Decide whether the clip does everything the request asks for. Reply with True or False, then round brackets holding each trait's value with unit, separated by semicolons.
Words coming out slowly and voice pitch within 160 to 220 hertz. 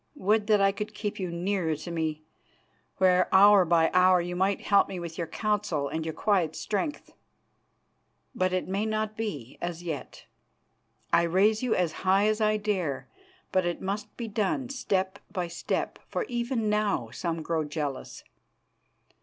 False (165 wpm; 190 Hz)